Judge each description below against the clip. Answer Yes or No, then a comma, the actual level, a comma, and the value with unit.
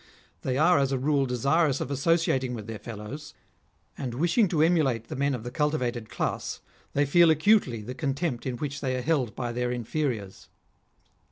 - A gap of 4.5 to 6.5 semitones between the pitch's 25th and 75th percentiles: No, average, 3.9 semitones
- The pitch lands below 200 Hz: Yes, low, 135 Hz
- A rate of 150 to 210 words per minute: Yes, average, 180 wpm